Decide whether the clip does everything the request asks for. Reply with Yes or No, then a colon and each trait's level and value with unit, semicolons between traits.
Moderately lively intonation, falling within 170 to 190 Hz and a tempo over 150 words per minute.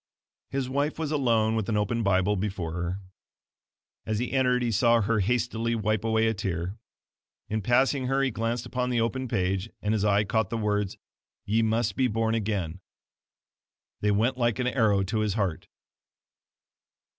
No: average, 3.1 semitones; low, 110 Hz; average, 170 wpm